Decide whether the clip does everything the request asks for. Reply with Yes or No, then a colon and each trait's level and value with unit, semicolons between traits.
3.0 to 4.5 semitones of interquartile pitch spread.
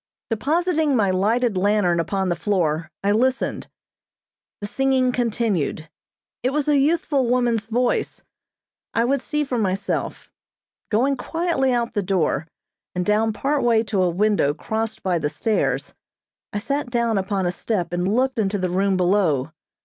No: average, 5.3 semitones